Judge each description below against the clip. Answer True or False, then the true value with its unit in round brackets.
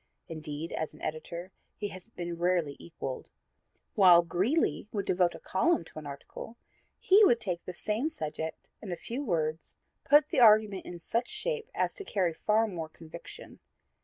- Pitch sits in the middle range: True (180 Hz)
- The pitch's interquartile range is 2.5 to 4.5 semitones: False (5.6 semitones)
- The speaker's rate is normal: True (175 wpm)